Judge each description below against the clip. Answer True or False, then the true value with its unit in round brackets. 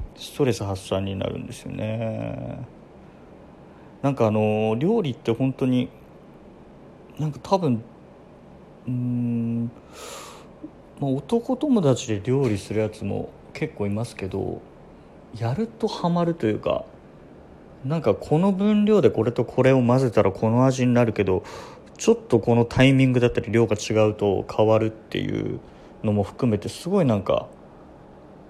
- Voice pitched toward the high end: False (120 Hz)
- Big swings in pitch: False (3.8 semitones)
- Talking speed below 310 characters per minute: True (270 characters per minute)